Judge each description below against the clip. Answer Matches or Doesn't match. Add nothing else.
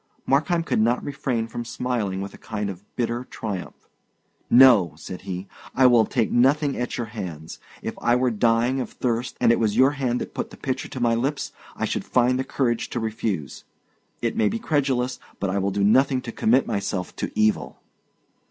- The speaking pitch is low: Matches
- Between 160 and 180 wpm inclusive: Doesn't match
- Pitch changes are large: Doesn't match